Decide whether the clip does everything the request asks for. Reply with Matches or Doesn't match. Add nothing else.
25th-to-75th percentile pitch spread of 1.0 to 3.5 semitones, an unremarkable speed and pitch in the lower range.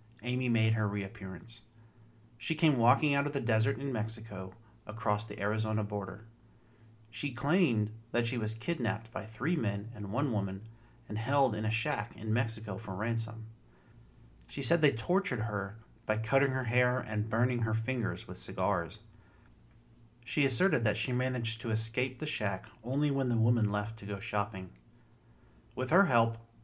Matches